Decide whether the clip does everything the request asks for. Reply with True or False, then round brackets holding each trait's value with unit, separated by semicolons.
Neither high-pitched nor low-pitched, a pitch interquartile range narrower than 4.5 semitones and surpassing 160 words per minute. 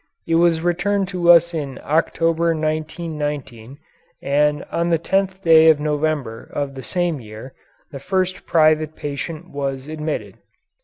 False (155 Hz; 2.8 semitones; 140 wpm)